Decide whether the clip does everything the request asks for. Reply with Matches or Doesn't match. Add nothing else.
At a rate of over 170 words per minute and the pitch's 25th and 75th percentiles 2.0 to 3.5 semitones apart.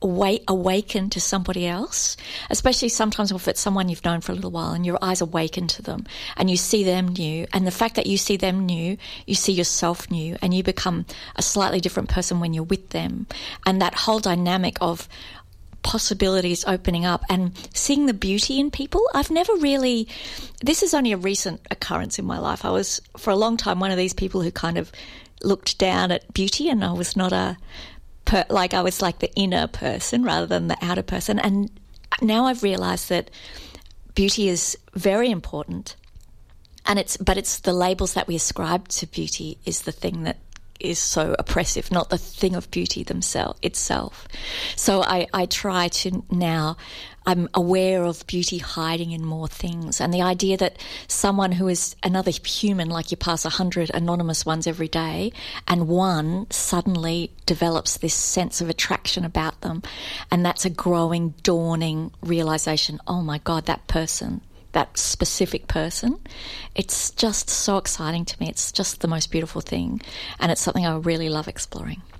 Matches